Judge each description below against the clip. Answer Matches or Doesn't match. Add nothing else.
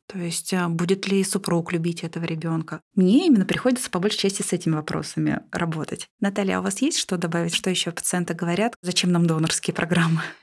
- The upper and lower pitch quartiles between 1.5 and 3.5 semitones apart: Matches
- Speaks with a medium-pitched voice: Matches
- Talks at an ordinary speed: Doesn't match